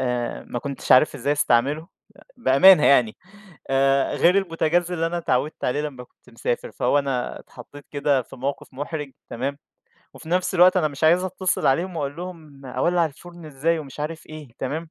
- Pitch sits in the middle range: Yes, medium, 150 Hz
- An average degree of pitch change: Yes, average, 3.8 semitones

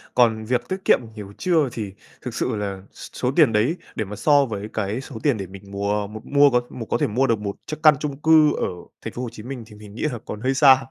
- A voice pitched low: Yes, low, 115 Hz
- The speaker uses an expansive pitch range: No, average, 4.7 semitones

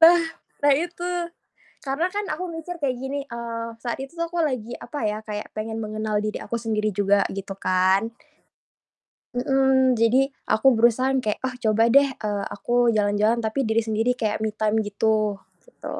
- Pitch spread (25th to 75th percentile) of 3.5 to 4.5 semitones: Yes, average, 3.9 semitones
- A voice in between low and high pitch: No, high, 230 Hz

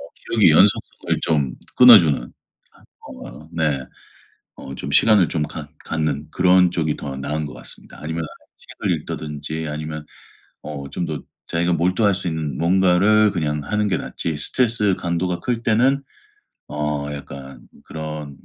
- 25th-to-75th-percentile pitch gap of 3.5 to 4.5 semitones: Yes, average, 3.8 semitones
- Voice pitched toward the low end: Yes, very low, 80 Hz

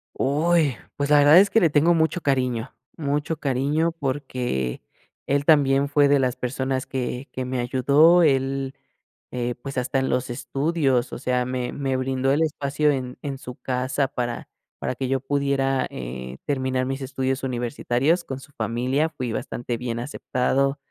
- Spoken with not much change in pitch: Yes, narrow, 2.2 semitones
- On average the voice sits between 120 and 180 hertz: Yes, low, 135 Hz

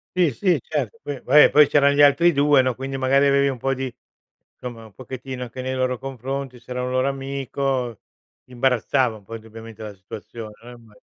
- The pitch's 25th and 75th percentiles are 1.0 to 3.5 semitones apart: Yes, narrow, 2.5 semitones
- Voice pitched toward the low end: Yes, low, 130 Hz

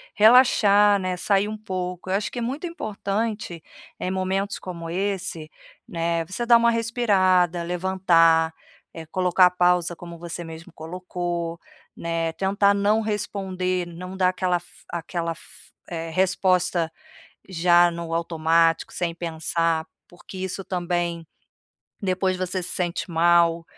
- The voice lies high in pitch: No, medium, 180 Hz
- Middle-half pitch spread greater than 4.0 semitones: No, narrow, 2.4 semitones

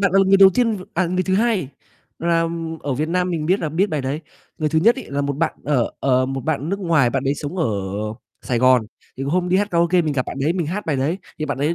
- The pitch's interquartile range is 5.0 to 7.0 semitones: No, average, 4.6 semitones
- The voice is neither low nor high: Yes, medium, 160 Hz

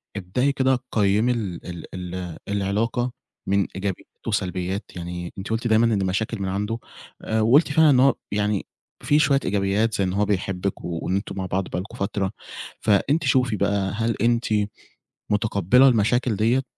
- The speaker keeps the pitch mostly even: No, average, 3.5 semitones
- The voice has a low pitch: Yes, low, 105 Hz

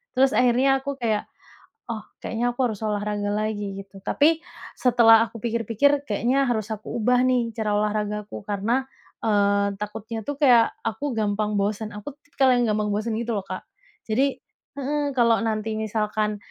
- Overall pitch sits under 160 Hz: No, high, 225 Hz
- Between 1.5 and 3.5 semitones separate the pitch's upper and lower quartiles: Yes, average, 3.0 semitones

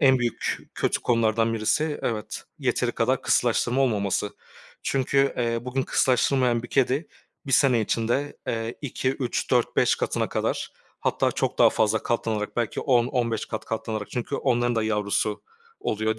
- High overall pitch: No, low, 120 Hz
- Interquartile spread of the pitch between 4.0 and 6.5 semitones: No, average, 2.8 semitones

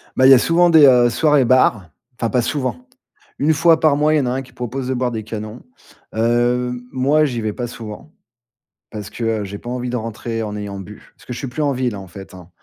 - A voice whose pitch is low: Yes, low, 125 Hz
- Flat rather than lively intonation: No, average, 3.7 semitones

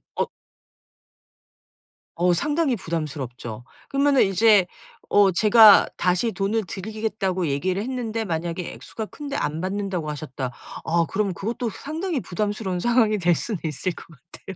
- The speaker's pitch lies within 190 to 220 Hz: Yes, high, 195 Hz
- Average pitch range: Yes, average, 4.7 semitones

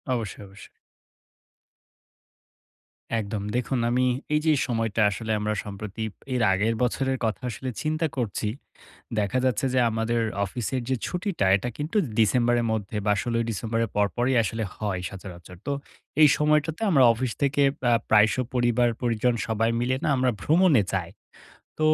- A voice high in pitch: No, low, 115 Hz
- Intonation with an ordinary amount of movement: Yes, average, 3.5 semitones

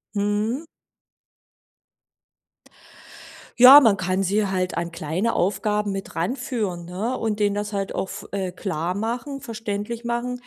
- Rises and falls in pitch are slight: No, average, 3.7 semitones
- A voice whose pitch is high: Yes, high, 205 Hz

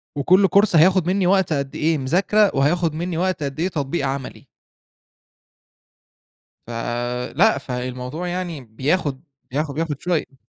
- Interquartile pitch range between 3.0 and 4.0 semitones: No, average, 5.1 semitones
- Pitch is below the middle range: No, medium, 155 Hz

